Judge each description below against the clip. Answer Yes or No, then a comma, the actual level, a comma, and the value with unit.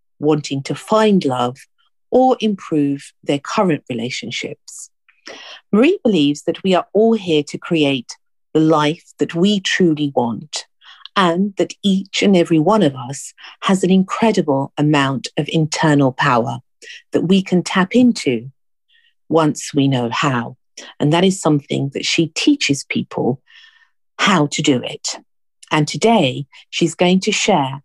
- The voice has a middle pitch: Yes, medium, 165 Hz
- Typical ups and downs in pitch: No, wide, 5.7 semitones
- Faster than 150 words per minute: No, average, 140 wpm